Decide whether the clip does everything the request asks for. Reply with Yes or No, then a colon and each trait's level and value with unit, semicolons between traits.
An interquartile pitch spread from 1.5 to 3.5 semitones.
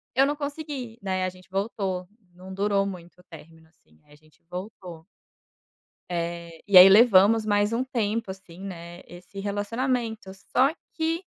No: average, 4.2 semitones